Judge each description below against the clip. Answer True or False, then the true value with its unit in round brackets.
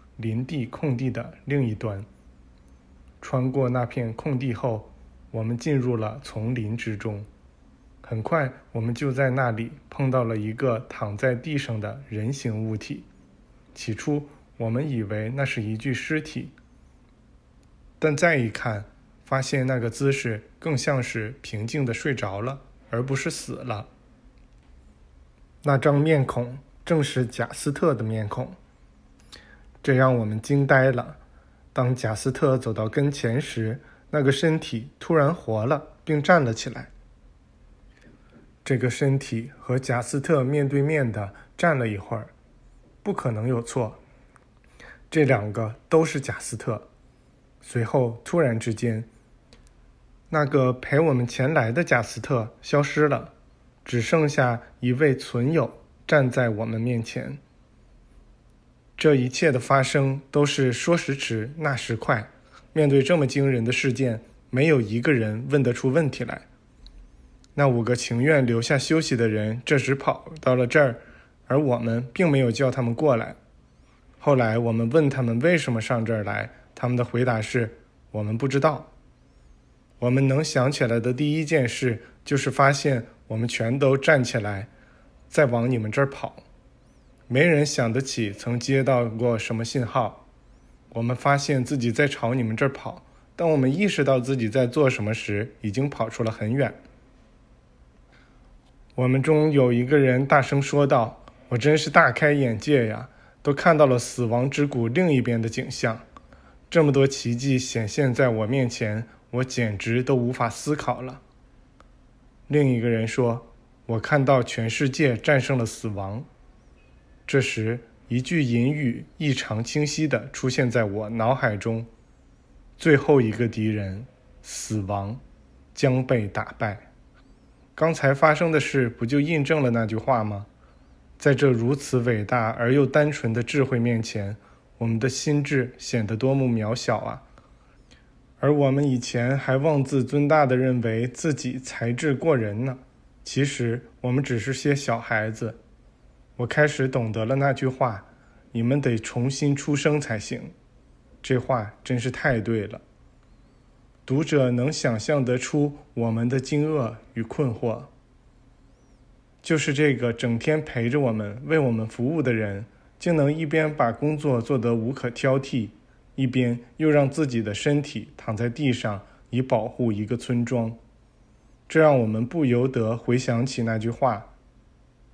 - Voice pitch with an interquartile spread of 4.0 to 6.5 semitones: False (3.5 semitones)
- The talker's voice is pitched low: True (125 Hz)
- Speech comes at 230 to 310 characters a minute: False (215 characters per minute)